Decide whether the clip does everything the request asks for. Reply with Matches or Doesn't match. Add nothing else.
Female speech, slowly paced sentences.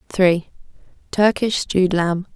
Matches